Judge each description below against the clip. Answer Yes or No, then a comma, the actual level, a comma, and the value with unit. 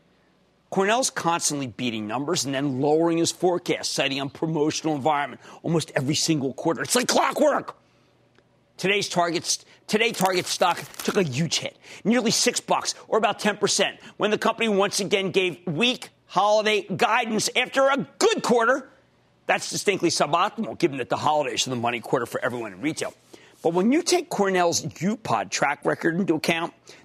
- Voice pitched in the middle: Yes, medium, 180 Hz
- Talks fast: No, average, 160 wpm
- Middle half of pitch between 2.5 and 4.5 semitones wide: No, average, 5.3 semitones